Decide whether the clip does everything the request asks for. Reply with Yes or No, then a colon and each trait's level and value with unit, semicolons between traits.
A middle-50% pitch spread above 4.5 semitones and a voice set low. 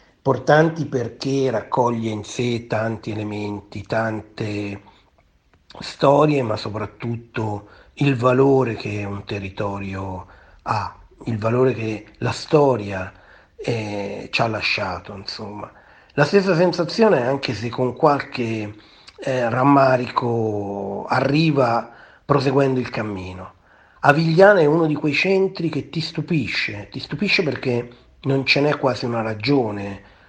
Yes: average, 5.1 semitones; low, 120 Hz